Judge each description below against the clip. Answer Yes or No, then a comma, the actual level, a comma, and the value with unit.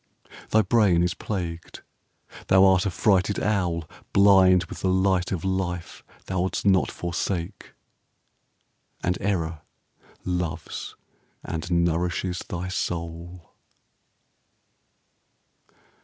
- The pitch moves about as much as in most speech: No, narrow, 1.8 semitones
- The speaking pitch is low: Yes, very low, 90 Hz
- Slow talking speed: Yes, slow, 95 wpm